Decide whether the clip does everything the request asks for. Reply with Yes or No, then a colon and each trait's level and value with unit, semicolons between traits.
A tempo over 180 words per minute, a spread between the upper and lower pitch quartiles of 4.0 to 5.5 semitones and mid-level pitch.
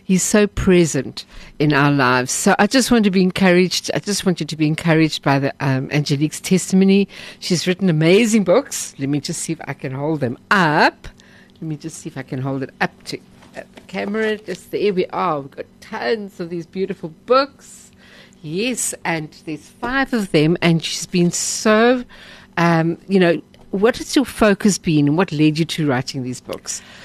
Yes: average, 200 wpm; average, 4.7 semitones; medium, 175 Hz